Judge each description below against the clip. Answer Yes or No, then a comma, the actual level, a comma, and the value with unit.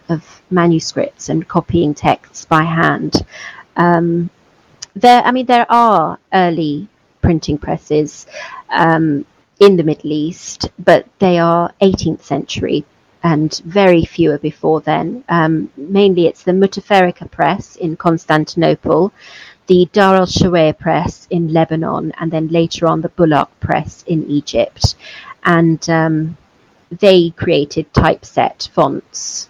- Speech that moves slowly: Yes, slow, 125 wpm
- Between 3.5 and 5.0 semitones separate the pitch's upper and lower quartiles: No, average, 2.7 semitones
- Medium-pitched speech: Yes, medium, 170 Hz